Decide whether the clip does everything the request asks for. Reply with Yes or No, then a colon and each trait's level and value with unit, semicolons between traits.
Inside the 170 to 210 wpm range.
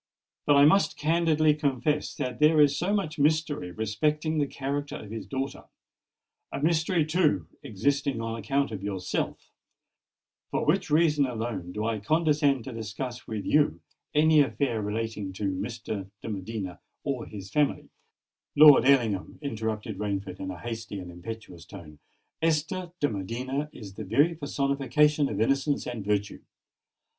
No: average, 145 wpm